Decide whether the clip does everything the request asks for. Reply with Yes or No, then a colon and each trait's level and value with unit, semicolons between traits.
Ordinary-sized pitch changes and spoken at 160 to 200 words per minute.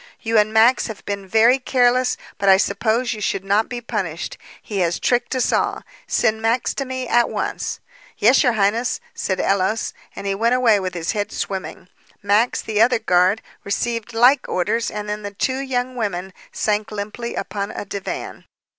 Yes: average, 3.3 semitones; average, 180 wpm